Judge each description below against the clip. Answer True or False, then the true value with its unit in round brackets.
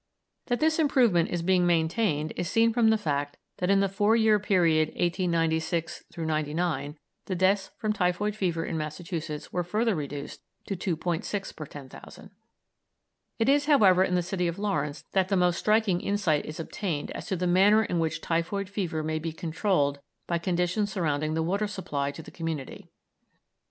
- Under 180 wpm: True (170 wpm)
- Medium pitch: True (175 Hz)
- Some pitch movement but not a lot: True (4.0 semitones)